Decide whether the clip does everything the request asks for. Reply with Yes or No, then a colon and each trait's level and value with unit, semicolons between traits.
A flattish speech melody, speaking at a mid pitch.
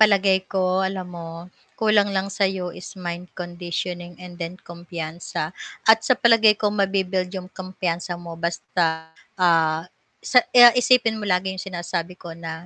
Yes: narrow, 2.2 semitones; medium, 180 Hz